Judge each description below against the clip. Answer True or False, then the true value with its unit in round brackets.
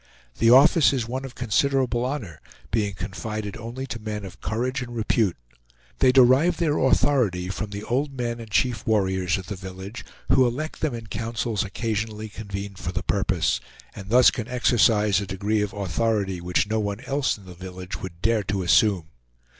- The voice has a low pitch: True (110 Hz)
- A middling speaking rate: True (180 wpm)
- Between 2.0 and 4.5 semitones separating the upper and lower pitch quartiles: True (4.0 semitones)